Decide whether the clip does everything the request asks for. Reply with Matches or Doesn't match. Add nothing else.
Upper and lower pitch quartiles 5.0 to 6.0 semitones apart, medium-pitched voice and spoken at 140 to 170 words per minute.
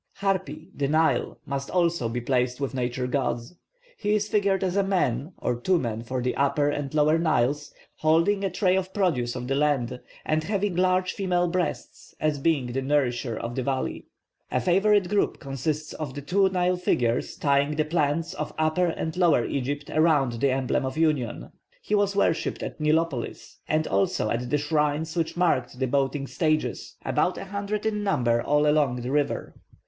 Doesn't match